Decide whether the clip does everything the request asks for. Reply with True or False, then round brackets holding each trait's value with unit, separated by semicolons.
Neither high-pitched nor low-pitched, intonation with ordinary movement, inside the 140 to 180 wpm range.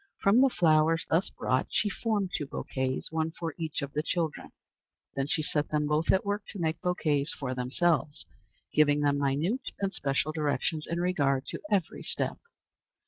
True (155 Hz; 3.5 semitones; 175 wpm)